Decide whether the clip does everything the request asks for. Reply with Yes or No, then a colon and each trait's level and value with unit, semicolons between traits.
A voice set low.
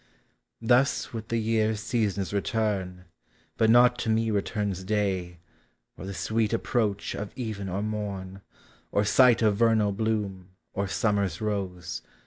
Yes: low, 105 Hz